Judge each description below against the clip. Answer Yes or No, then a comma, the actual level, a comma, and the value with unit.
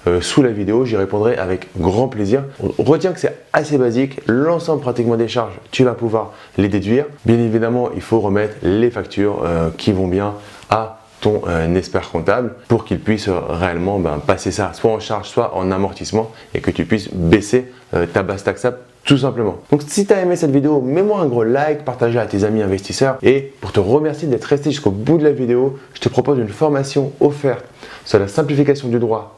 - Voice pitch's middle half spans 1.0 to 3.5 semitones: No, average, 5.1 semitones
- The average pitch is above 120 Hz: No, low, 115 Hz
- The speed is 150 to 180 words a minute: No, average, 195 wpm